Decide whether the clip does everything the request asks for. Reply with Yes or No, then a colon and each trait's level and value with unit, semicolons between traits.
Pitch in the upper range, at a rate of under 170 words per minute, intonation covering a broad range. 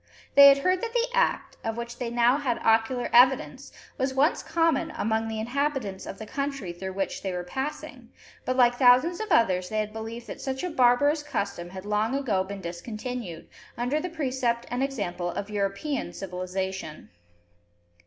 No: high, 240 Hz; average, 175 wpm; wide, 5.7 semitones